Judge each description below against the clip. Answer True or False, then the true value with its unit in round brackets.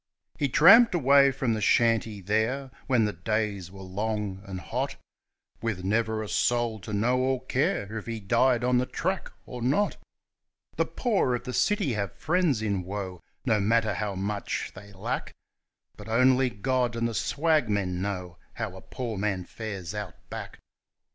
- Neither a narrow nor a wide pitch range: True (4.2 semitones)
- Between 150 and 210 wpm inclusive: True (165 wpm)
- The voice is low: True (110 Hz)